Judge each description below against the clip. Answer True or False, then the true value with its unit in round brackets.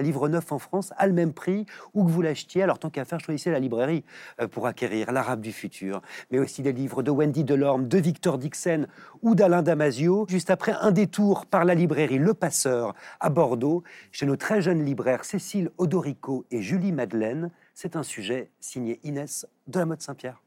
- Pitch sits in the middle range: True (160 Hz)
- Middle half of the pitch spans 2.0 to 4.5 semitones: False (5.3 semitones)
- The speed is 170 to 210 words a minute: True (195 wpm)